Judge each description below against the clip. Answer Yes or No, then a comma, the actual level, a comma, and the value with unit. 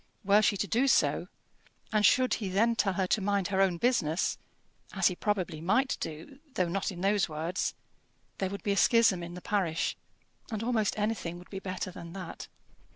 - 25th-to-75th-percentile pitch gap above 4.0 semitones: No, average, 3.0 semitones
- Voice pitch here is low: No, high, 195 Hz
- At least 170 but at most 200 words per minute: Yes, average, 195 wpm